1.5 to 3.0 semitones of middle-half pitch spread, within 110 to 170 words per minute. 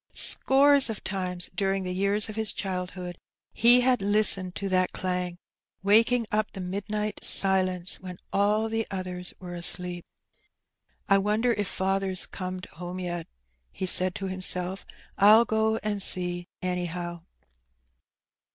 Yes: narrow, 2.6 semitones; average, 140 wpm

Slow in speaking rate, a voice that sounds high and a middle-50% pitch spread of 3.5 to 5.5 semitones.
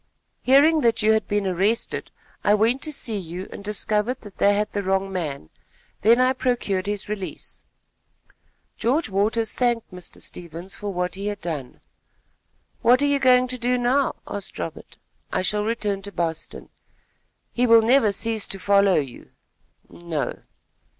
No: average, 160 wpm; high, 210 Hz; average, 4.0 semitones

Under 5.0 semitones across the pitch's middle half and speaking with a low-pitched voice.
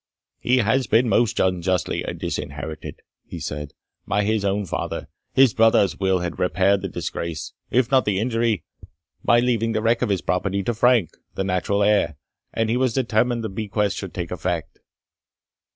Yes: average, 4.1 semitones; low, 105 Hz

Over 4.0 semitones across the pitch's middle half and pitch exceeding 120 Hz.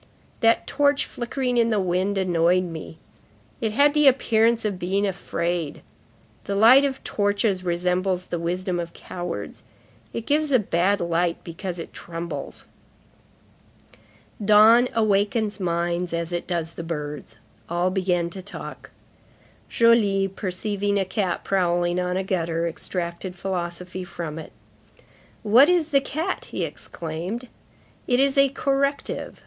Yes: average, 4.7 semitones; high, 190 Hz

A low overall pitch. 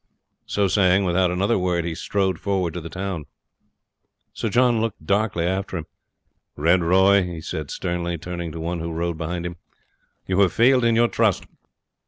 Yes: very low, 90 Hz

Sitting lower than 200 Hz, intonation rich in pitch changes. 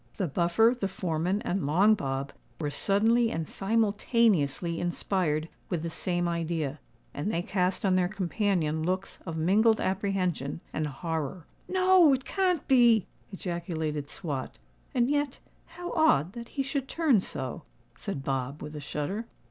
Yes: medium, 185 Hz; wide, 6.1 semitones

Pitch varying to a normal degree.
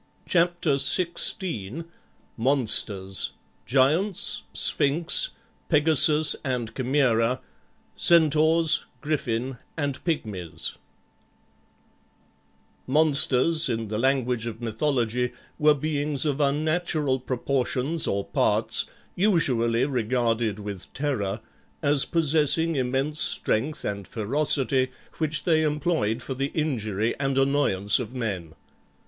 Yes: average, 4.9 semitones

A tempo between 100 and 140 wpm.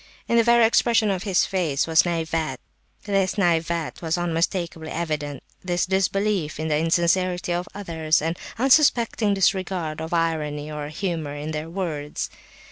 Yes: slow, 135 wpm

